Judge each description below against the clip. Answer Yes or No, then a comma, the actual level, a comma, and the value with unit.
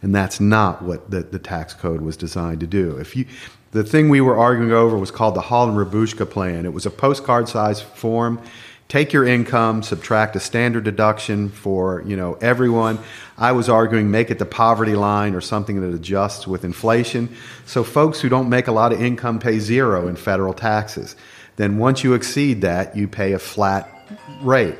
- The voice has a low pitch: Yes, low, 110 Hz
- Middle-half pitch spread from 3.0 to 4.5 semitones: Yes, average, 3.6 semitones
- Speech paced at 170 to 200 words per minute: Yes, average, 195 wpm